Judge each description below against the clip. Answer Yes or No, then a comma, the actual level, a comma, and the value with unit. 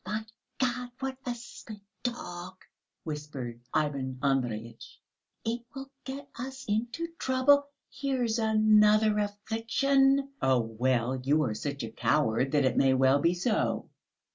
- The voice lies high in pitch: Yes, high, 210 Hz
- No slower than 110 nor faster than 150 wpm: Yes, average, 140 wpm